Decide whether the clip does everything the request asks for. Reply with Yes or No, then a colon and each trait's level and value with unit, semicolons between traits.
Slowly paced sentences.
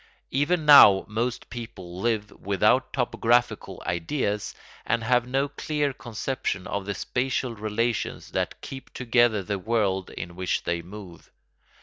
Yes: slow, 130 wpm